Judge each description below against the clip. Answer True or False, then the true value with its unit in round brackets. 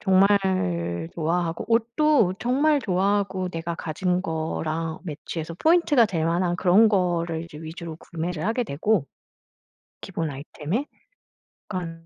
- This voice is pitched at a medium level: True (175 Hz)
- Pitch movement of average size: True (3.9 semitones)